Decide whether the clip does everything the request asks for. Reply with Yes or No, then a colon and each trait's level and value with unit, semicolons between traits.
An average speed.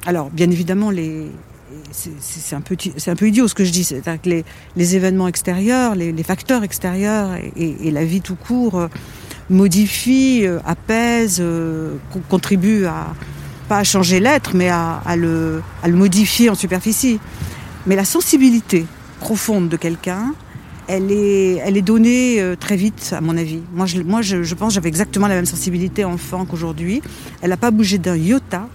Yes: average, 185 wpm